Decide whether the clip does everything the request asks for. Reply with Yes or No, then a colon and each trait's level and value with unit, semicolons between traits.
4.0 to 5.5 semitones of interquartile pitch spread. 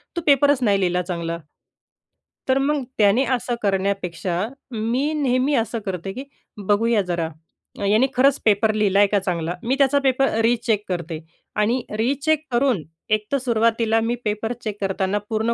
Yes: average, 4.5 semitones